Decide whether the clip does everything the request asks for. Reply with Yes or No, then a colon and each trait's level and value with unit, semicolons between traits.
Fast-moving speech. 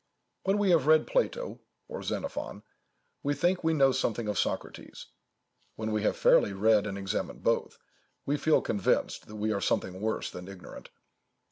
No: average, 165 wpm